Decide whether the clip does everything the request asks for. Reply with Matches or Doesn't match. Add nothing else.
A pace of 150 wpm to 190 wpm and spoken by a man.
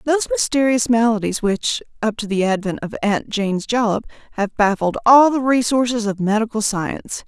Doesn't match